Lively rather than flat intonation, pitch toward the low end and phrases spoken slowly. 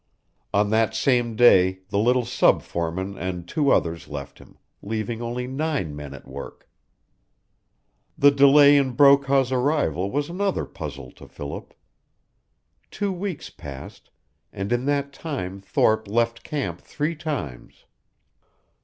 Yes: wide, 6.9 semitones; low, 120 Hz; slow, 130 wpm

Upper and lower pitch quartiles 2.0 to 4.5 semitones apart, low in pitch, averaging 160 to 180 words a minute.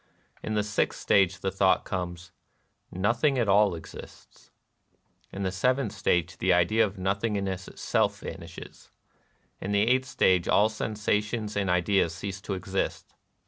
No: narrow, 2.4 semitones; low, 100 Hz; average, 145 wpm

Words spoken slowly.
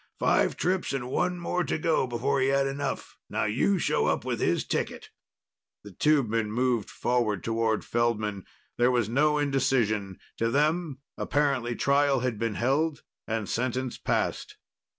No: average, 150 wpm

